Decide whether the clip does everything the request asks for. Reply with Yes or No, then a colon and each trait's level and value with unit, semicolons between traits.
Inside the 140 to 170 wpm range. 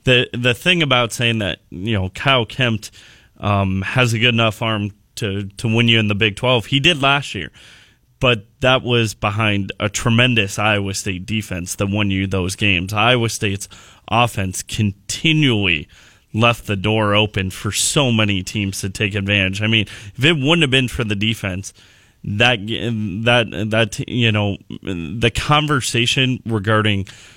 Yes: average, 165 wpm